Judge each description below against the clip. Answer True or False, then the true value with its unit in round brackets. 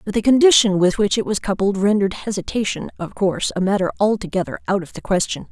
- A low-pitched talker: False (200 Hz)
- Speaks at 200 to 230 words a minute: True (205 wpm)